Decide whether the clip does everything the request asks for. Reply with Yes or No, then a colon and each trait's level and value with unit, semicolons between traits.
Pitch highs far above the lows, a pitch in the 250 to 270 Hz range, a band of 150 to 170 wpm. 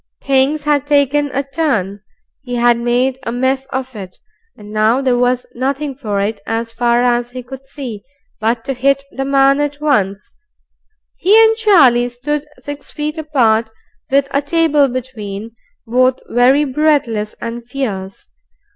No: average, 3.3 semitones; very high, 260 Hz; average, 155 wpm